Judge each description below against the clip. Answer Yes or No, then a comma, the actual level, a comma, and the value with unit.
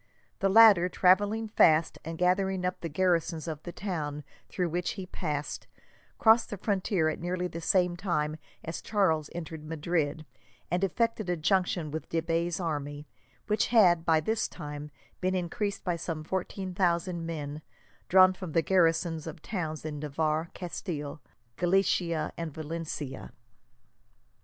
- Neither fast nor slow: Yes, average, 145 wpm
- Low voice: No, medium, 170 Hz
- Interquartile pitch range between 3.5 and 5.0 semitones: No, average, 2.9 semitones